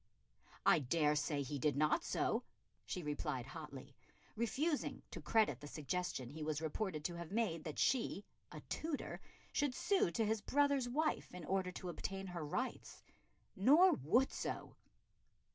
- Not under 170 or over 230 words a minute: No, average, 155 wpm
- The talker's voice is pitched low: No, medium, 175 Hz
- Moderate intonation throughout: No, wide, 7.7 semitones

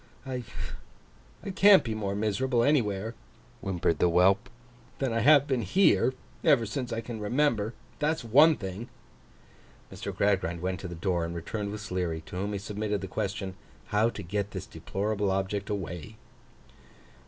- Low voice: Yes, low, 105 Hz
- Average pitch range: Yes, average, 3.7 semitones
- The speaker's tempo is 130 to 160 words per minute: Yes, average, 155 wpm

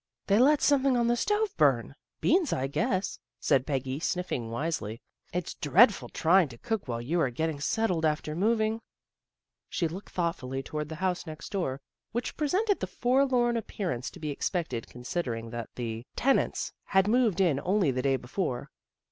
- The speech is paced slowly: No, average, 170 wpm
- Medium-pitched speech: Yes, medium, 175 Hz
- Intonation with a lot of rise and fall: Yes, wide, 8.9 semitones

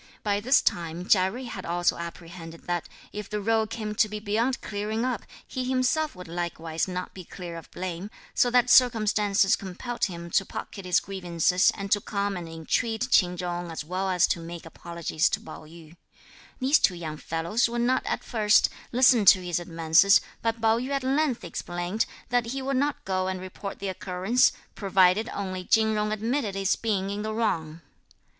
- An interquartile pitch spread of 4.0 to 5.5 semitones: Yes, average, 4.4 semitones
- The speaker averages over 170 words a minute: Yes, average, 190 wpm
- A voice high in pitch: Yes, high, 195 Hz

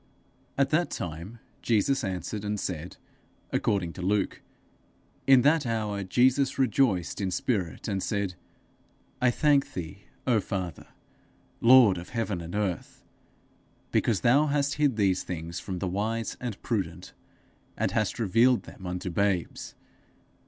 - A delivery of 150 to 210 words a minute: No, average, 140 wpm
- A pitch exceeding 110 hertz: No, low, 105 Hz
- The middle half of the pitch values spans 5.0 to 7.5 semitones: Yes, average, 5.3 semitones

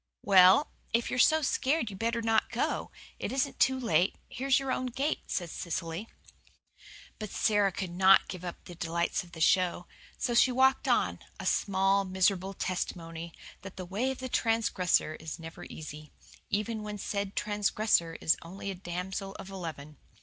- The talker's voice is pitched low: No, high, 195 Hz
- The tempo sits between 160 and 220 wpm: Yes, average, 170 wpm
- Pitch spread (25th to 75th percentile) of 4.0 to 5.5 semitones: Yes, average, 4.5 semitones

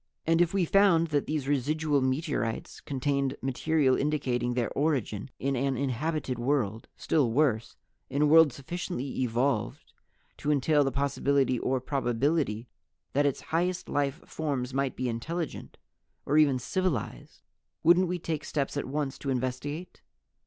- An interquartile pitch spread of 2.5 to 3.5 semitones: Yes, average, 3.2 semitones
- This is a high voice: No, medium, 140 Hz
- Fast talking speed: No, average, 145 wpm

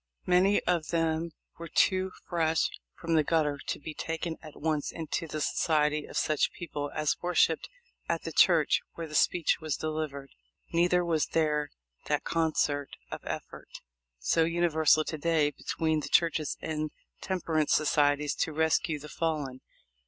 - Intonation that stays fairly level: Yes, narrow, 1.8 semitones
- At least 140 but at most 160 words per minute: Yes, average, 150 wpm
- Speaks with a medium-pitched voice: Yes, medium, 160 Hz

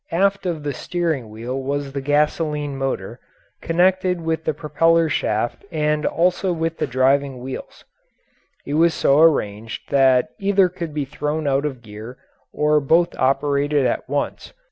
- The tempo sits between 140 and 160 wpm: Yes, average, 150 wpm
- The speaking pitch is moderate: Yes, medium, 150 Hz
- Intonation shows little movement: No, average, 3.5 semitones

